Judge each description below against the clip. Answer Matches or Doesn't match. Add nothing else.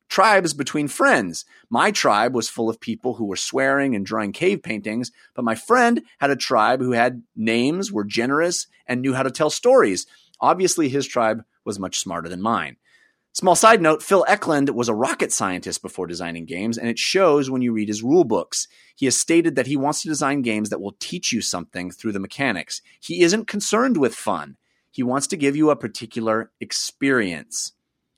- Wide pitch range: Matches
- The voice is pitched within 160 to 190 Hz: Doesn't match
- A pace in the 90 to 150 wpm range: Doesn't match